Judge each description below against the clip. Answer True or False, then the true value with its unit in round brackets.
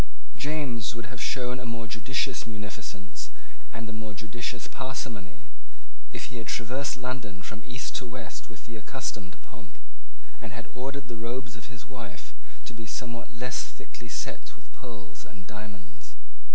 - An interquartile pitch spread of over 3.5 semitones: False (3.0 semitones)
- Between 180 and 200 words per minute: False (160 wpm)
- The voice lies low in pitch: True (115 Hz)